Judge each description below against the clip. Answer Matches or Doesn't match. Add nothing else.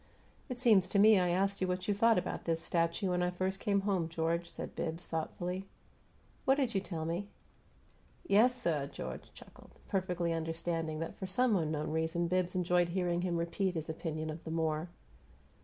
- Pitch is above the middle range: Doesn't match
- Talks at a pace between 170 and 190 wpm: Matches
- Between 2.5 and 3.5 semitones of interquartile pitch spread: Matches